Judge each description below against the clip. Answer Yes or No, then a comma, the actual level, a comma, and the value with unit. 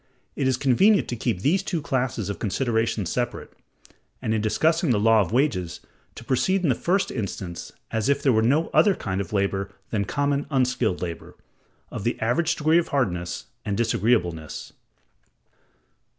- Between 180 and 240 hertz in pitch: No, low, 120 Hz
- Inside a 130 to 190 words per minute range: Yes, average, 165 wpm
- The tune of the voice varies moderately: No, wide, 5.9 semitones